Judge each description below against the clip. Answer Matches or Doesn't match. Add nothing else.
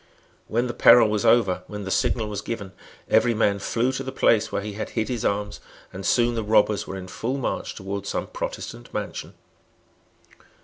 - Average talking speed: Matches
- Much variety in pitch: Doesn't match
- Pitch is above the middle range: Doesn't match